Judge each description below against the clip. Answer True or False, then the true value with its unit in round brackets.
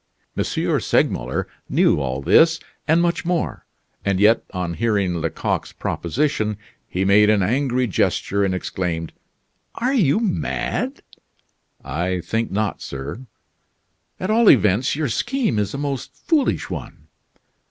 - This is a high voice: False (105 Hz)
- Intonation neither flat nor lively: False (8.2 semitones)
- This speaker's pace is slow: True (130 wpm)